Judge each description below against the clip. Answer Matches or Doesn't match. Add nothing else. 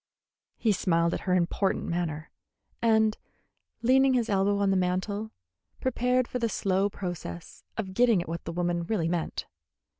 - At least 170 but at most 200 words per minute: Doesn't match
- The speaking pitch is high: Matches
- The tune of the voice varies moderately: Matches